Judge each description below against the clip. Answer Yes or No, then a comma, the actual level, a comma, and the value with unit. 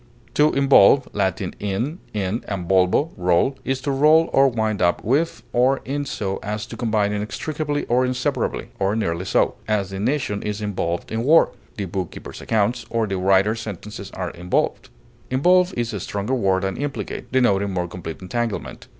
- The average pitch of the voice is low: Yes, low, 105 Hz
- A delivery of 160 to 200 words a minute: Yes, average, 170 wpm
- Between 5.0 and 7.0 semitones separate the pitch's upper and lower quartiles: Yes, wide, 5.4 semitones